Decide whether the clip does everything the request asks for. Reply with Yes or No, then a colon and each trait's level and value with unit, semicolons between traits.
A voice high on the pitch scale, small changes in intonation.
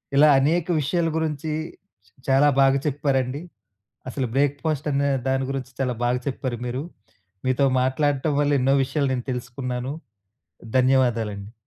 No: low, 135 Hz; narrow, 2.2 semitones